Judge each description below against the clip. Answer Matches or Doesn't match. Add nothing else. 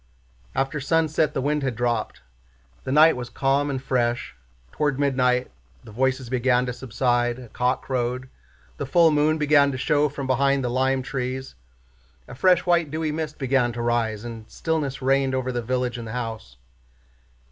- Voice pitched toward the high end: Doesn't match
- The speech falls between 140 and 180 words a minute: Matches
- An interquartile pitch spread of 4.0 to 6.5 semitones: Doesn't match